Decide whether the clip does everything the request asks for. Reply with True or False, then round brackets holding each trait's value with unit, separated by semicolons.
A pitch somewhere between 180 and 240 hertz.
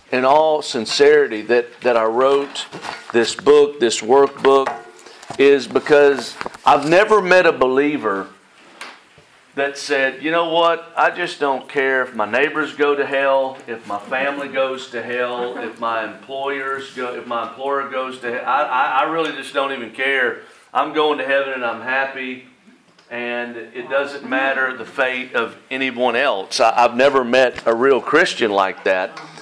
False (135 Hz)